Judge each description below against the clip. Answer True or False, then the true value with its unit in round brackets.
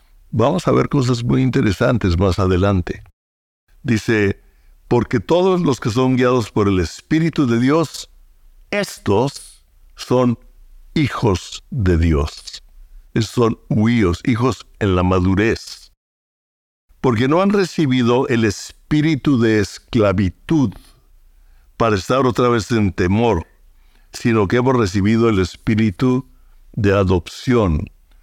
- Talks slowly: True (115 wpm)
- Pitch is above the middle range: False (110 Hz)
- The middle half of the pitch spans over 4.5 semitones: True (5.4 semitones)